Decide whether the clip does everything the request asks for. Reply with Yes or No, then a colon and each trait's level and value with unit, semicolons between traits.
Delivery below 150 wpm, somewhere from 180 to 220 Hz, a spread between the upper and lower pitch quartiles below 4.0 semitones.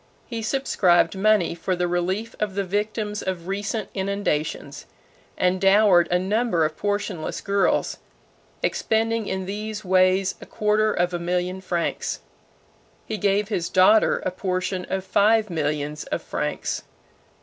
Yes: average, 140 wpm; high, 190 Hz; average, 2.8 semitones